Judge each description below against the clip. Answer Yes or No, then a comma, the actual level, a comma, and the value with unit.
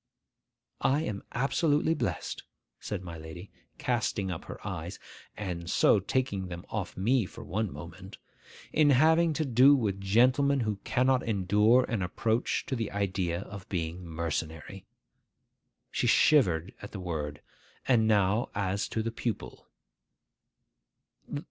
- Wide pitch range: Yes, wide, 5.8 semitones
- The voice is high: No, low, 100 Hz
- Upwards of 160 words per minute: No, slow, 135 wpm